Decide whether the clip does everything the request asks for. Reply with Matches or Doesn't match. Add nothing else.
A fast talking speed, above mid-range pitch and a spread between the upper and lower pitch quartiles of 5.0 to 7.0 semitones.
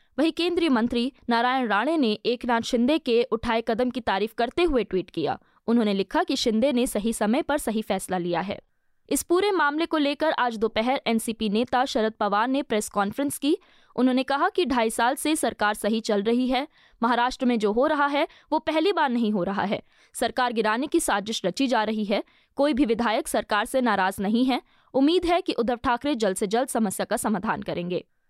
Doesn't match